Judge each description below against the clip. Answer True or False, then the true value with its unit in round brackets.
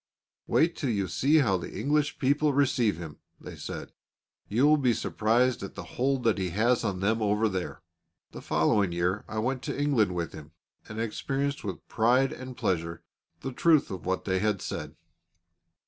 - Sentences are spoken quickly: False (180 wpm)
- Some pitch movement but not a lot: False (6.0 semitones)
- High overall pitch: False (110 Hz)